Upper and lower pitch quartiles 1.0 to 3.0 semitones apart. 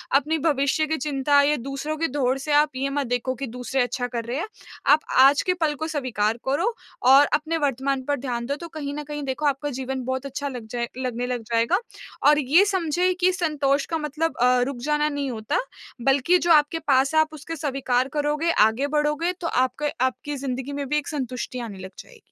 Yes: average, 2.7 semitones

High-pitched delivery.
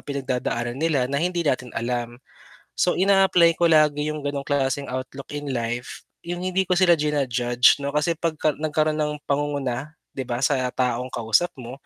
No: medium, 145 Hz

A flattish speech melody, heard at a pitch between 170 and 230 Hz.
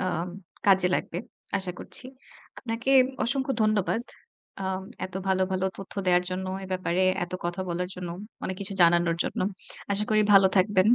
Yes: narrow, 2.1 semitones; high, 190 Hz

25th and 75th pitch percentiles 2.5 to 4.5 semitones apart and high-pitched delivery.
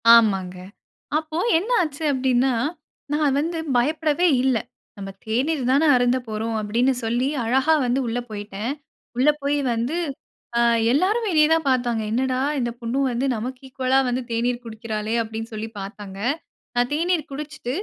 Yes: average, 4.2 semitones; very high, 250 Hz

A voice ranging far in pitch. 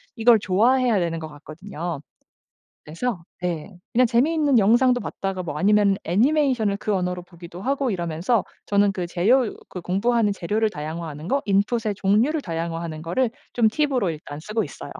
Yes: wide, 5.8 semitones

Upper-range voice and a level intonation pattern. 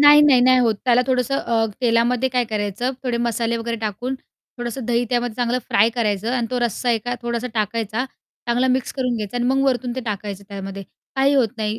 Yes: high, 240 Hz; narrow, 2.1 semitones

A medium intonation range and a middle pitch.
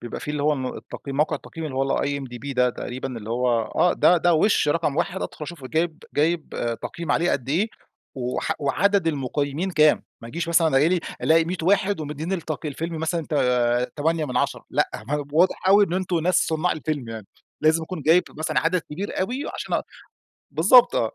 Yes: average, 3.9 semitones; medium, 155 Hz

